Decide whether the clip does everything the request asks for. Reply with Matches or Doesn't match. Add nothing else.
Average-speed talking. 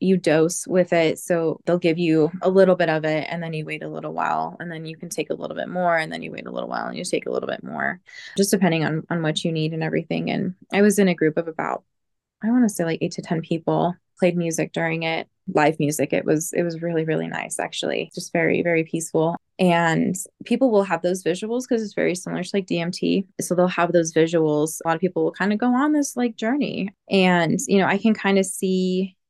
Doesn't match